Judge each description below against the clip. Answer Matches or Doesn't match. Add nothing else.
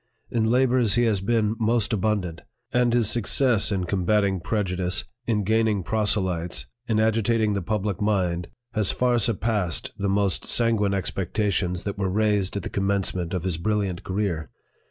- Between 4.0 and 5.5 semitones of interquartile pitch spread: Doesn't match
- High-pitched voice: Doesn't match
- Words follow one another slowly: Doesn't match